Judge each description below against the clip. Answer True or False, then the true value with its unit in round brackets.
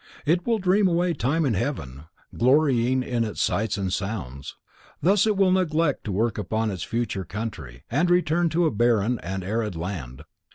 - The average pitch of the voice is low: True (120 Hz)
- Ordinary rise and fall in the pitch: False (8.9 semitones)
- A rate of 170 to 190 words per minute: True (175 wpm)